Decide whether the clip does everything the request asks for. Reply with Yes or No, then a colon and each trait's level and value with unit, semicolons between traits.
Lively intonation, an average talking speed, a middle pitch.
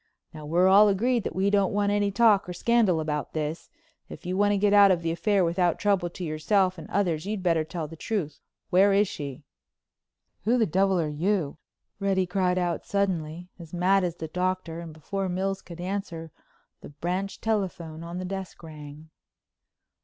No: average, 3.3 semitones; average, 190 wpm; medium, 180 Hz